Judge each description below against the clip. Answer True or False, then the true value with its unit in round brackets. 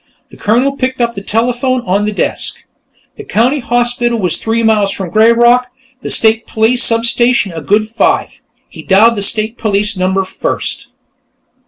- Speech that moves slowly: False (160 wpm)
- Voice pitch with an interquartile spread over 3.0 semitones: False (2.7 semitones)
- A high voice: True (225 Hz)